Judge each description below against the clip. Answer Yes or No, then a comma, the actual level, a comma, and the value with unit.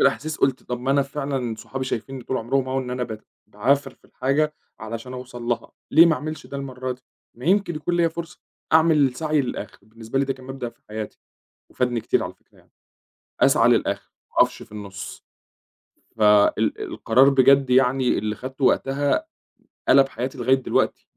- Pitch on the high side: No, low, 130 Hz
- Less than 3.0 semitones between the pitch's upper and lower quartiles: Yes, narrow, 2.5 semitones